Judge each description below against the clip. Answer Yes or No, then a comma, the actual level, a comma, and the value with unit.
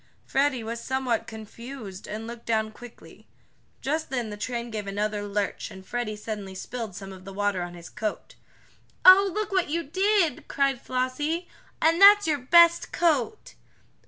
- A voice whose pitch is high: Yes, high, 240 Hz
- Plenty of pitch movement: Yes, wide, 6.8 semitones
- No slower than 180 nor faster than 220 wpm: No, average, 160 wpm